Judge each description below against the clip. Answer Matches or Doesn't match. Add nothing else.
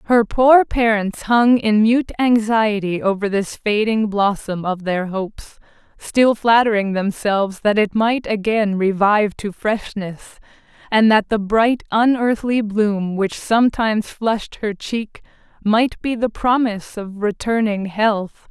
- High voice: Matches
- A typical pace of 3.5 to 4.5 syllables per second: Matches